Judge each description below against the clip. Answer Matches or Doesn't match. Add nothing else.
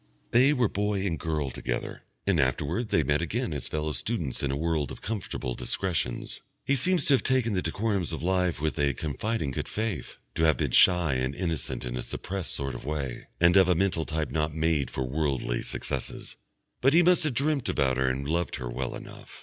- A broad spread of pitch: Matches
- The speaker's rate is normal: Doesn't match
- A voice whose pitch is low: Matches